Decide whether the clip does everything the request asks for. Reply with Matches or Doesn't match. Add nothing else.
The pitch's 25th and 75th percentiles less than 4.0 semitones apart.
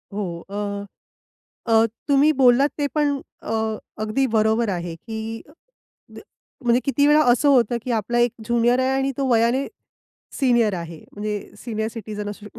Matches